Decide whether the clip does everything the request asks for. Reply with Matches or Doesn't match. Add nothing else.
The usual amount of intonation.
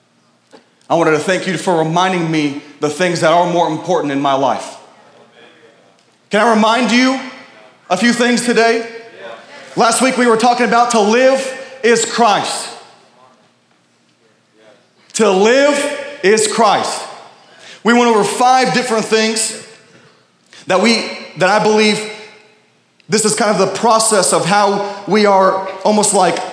Matches